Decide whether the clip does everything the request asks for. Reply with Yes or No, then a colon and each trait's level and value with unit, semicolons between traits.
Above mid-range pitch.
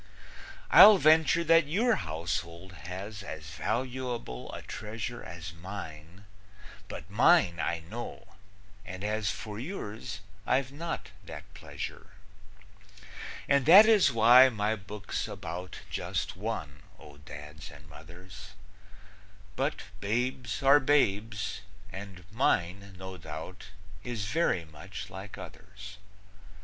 No: low, 100 Hz